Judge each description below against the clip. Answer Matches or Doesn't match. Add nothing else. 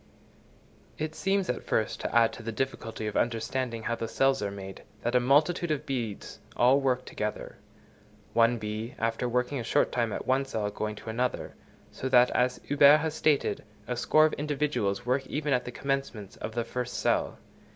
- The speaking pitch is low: Matches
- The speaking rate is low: Doesn't match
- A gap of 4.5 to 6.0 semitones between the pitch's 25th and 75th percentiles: Doesn't match